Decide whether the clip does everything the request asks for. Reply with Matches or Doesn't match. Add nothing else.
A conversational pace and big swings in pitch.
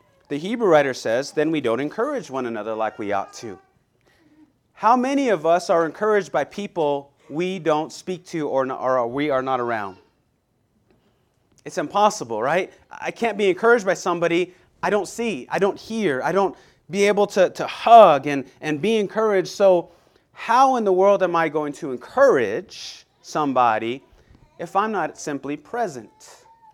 Matches